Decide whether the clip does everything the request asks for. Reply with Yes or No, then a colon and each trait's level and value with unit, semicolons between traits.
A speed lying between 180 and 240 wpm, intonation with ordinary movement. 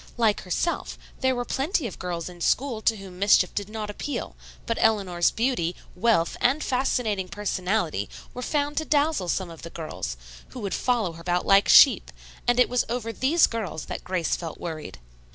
No: average, 185 wpm; wide, 5.7 semitones